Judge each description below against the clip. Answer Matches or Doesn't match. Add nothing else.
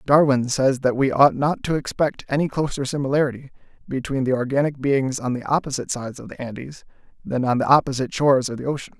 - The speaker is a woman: Doesn't match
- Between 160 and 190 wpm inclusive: Doesn't match